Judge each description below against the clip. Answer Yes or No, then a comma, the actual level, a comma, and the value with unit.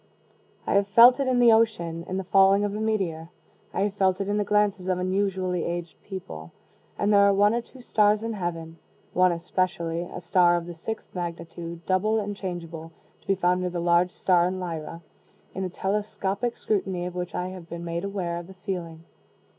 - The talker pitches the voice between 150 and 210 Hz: Yes, medium, 185 Hz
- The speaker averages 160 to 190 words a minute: No, fast, 205 wpm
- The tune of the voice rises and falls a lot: No, average, 2.8 semitones